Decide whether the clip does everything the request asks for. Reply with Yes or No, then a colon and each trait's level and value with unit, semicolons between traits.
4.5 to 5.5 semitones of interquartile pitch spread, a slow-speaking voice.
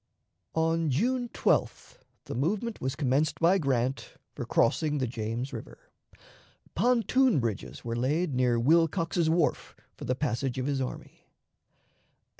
Yes: average, 5.0 semitones; slow, 130 wpm